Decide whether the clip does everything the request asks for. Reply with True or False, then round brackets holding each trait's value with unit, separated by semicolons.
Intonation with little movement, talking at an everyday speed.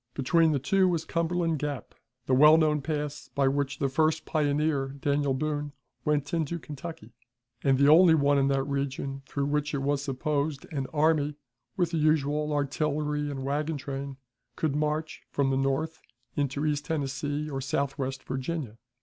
True (2.0 semitones; 165 wpm)